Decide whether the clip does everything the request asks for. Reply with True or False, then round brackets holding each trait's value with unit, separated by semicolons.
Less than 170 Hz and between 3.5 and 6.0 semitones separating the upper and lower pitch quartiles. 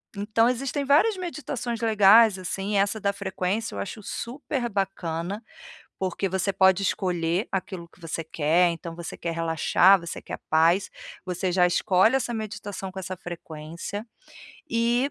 False (195 Hz; 4.3 semitones)